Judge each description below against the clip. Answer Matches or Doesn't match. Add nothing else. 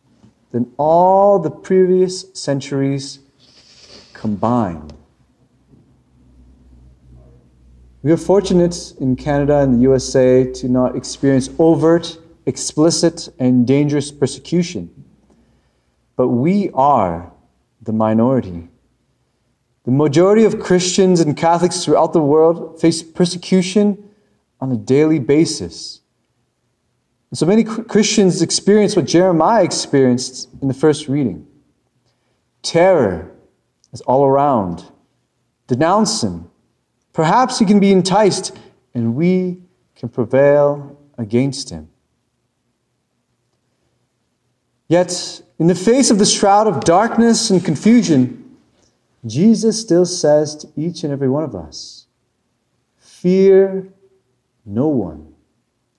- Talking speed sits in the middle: Doesn't match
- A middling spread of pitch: Doesn't match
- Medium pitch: Matches